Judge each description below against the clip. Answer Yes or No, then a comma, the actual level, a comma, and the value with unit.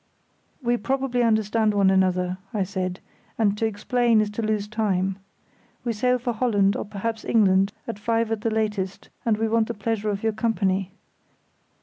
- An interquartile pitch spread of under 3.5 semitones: Yes, narrow, 2.5 semitones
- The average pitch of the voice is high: Yes, high, 215 Hz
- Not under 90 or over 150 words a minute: No, average, 170 wpm